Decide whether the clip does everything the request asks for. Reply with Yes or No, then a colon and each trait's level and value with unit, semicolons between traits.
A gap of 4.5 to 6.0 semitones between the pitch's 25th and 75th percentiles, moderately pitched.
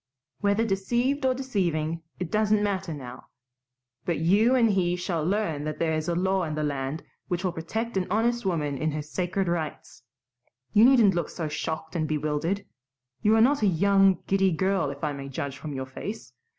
Yes: average, 4.8 semitones; medium, 175 Hz